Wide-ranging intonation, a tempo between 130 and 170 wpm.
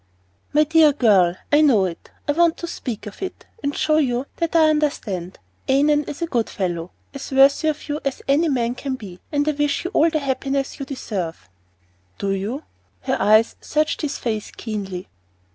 No: wide, 6.1 semitones; average, 195 wpm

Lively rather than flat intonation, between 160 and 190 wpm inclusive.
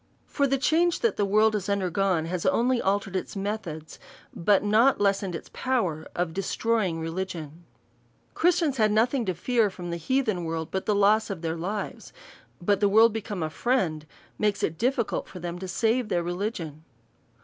No: average, 4.5 semitones; average, 180 wpm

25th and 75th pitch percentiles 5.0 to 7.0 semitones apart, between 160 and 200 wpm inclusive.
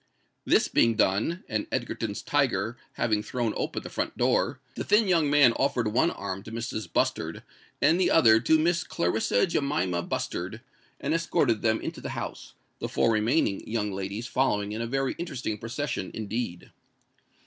Yes: average, 5.3 semitones; average, 165 wpm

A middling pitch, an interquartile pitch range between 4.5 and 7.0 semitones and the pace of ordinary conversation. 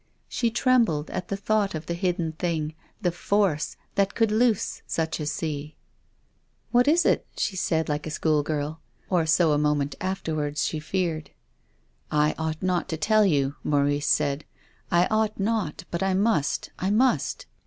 Yes: medium, 165 Hz; average, 4.8 semitones; average, 185 wpm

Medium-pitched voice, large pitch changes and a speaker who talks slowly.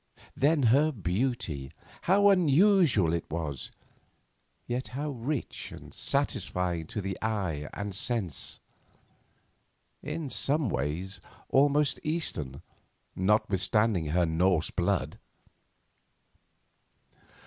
No: low, 105 Hz; wide, 8.5 semitones; slow, 85 wpm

